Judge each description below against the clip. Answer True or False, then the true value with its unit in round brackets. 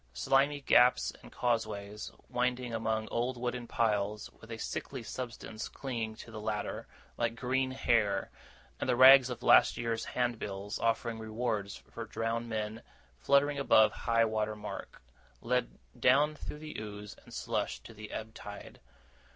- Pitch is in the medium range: False (115 Hz)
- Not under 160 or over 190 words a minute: False (150 wpm)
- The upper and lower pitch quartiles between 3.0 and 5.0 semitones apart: False (2.6 semitones)